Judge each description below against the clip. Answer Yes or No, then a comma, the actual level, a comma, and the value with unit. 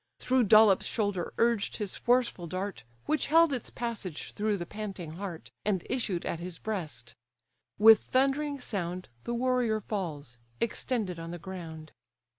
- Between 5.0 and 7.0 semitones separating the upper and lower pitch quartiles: Yes, average, 5.3 semitones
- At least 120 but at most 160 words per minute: Yes, average, 145 wpm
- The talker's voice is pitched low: No, high, 205 Hz